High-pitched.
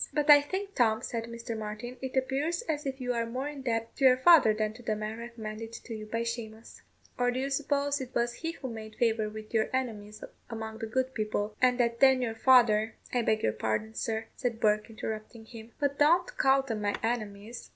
Yes: high, 235 Hz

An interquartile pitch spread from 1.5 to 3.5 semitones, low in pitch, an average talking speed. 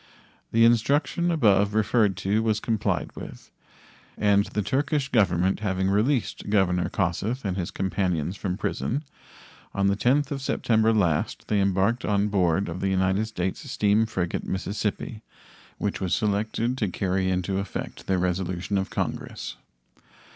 Yes: average, 2.9 semitones; low, 100 Hz; average, 145 wpm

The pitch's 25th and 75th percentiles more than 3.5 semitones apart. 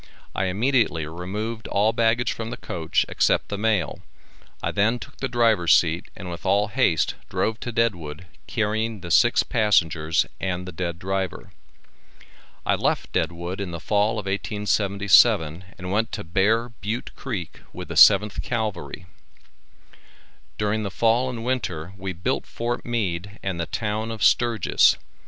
Yes: average, 4.0 semitones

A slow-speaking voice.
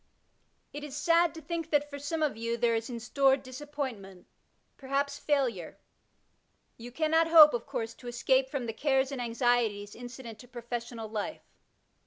No: average, 165 wpm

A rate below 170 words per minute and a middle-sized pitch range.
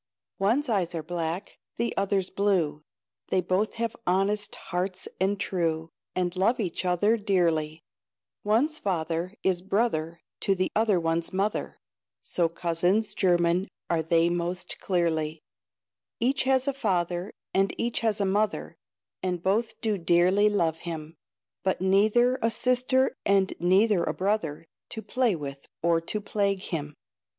Yes: average, 140 wpm; average, 3.8 semitones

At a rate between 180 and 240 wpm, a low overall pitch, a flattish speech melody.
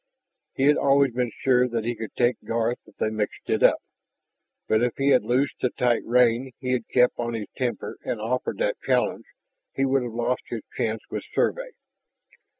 Yes: average, 195 wpm; low, 125 Hz; narrow, 2.1 semitones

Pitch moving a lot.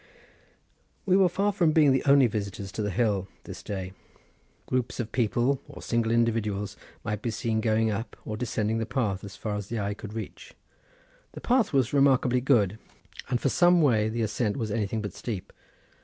No: average, 3.6 semitones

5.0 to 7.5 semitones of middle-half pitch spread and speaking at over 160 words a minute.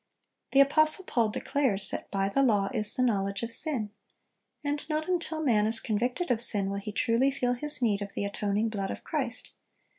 Yes: average, 5.3 semitones; average, 200 wpm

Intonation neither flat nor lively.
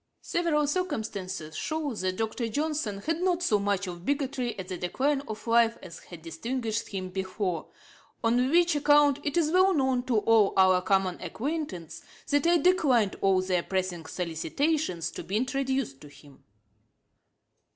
No: wide, 7.7 semitones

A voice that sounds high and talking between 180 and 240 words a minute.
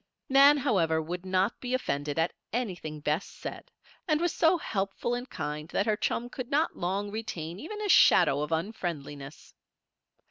No: high, 195 Hz; average, 165 wpm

